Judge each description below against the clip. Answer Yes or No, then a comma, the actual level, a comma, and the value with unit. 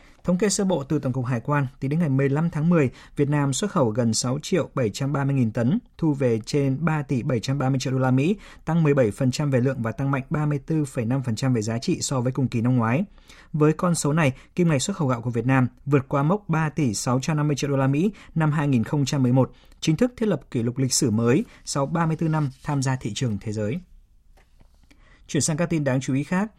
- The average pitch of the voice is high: No, medium, 140 Hz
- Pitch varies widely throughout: No, average, 3.7 semitones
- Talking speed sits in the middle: Yes, average, 230 wpm